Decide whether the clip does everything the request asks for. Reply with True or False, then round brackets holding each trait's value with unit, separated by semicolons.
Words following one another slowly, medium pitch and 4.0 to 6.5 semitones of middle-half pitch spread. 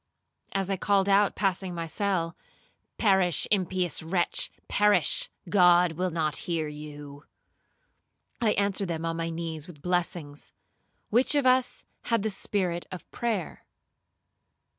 False (120 wpm; 180 Hz; 3.4 semitones)